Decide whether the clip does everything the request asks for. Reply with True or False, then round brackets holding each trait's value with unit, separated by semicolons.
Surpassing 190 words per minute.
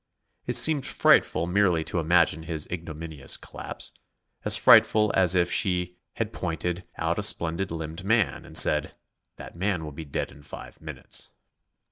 False (155 wpm)